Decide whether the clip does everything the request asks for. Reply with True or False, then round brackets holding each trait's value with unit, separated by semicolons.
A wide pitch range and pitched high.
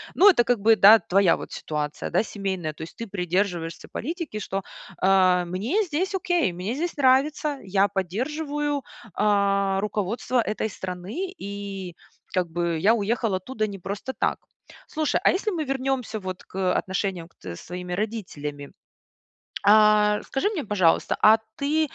True (6.2 semitones; 205 Hz)